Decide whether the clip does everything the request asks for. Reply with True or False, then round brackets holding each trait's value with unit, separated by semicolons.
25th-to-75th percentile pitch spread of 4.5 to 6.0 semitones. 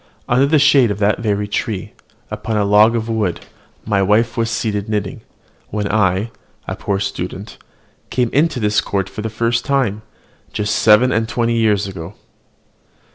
False (2.4 semitones)